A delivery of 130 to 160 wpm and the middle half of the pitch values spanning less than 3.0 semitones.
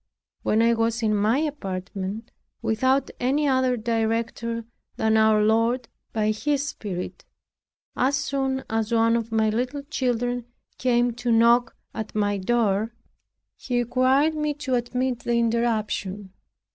Yes: slow, 135 wpm; narrow, 2.6 semitones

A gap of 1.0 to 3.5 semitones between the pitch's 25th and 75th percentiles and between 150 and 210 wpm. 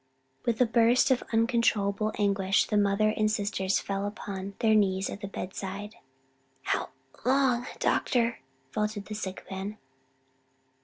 No: narrow, 2.4 semitones; slow, 135 wpm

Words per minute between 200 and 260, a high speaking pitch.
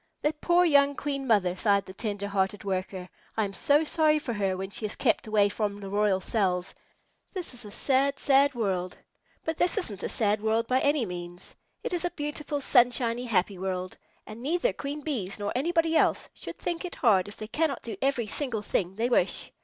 Yes: fast, 205 wpm; high, 225 Hz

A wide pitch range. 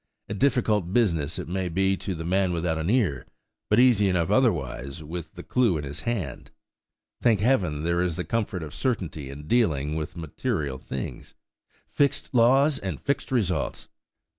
Yes: wide, 6.7 semitones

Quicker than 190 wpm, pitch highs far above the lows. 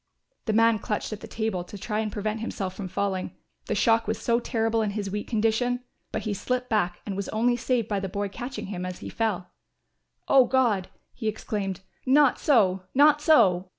No: average, 200 wpm; average, 3.2 semitones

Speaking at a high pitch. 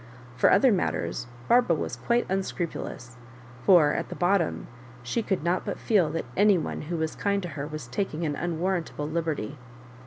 No: medium, 170 Hz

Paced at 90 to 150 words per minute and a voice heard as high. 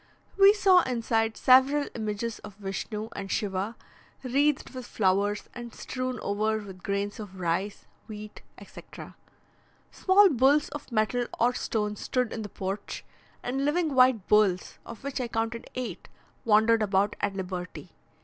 Yes: average, 145 wpm; high, 220 Hz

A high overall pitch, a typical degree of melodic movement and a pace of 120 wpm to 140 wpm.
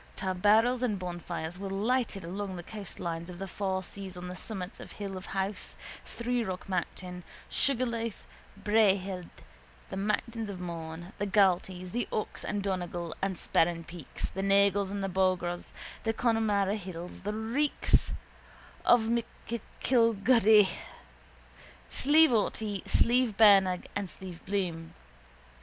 Yes: high, 195 Hz; average, 3.4 semitones; slow, 135 wpm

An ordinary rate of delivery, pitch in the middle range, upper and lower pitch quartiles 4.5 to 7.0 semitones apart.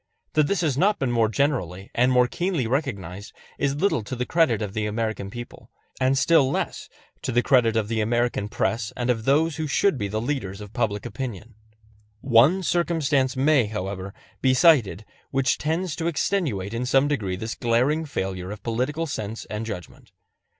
No: average, 180 wpm; low, 125 Hz; average, 5.2 semitones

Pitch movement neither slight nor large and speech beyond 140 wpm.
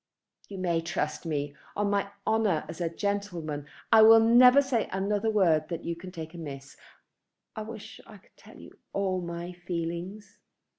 Yes: average, 4.1 semitones; average, 165 wpm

